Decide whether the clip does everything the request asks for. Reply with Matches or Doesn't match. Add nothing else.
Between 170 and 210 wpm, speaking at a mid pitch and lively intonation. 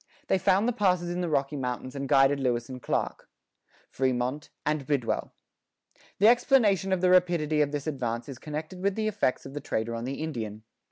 Matches